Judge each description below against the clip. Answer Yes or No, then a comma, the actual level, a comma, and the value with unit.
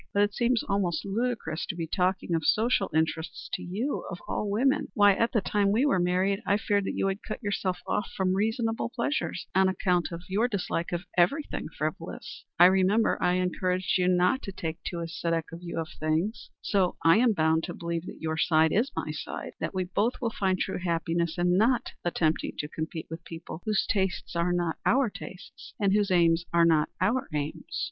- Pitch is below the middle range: No, medium, 185 Hz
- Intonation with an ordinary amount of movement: Yes, average, 3.6 semitones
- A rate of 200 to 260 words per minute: Yes, fast, 205 wpm